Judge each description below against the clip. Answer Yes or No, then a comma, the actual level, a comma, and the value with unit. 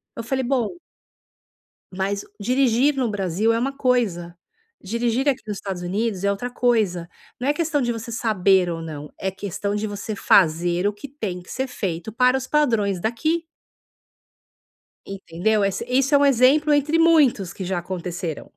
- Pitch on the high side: Yes, high, 220 Hz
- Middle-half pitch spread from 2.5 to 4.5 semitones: No, wide, 5.4 semitones